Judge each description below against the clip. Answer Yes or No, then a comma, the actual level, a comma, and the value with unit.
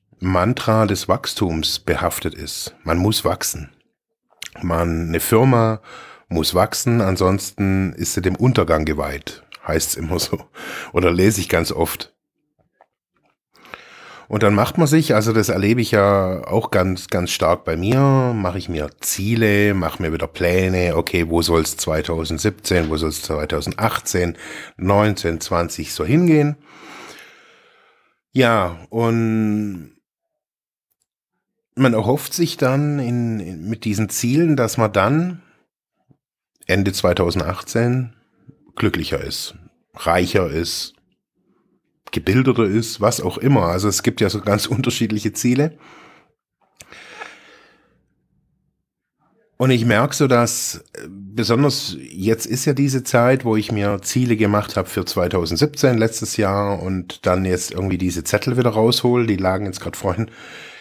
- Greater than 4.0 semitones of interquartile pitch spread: Yes, average, 4.9 semitones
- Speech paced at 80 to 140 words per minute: Yes, average, 130 wpm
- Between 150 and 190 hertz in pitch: No, low, 105 Hz